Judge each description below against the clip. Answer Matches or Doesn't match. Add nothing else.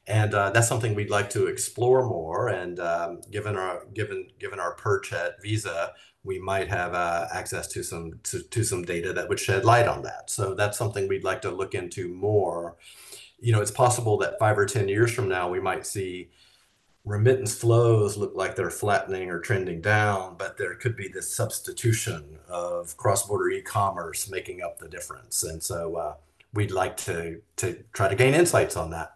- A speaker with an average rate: Matches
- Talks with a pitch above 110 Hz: Doesn't match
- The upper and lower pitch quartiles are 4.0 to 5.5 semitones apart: Matches